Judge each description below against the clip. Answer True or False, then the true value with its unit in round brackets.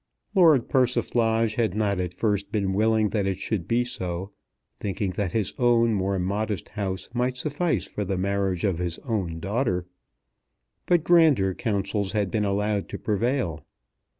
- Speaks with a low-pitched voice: True (105 Hz)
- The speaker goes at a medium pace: True (155 wpm)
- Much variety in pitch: False (3.4 semitones)